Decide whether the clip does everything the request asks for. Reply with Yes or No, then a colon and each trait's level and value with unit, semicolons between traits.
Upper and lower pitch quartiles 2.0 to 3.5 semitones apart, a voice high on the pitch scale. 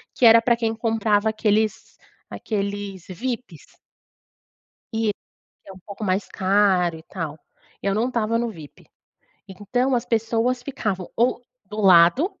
Yes: average, 3.2 semitones; high, 215 Hz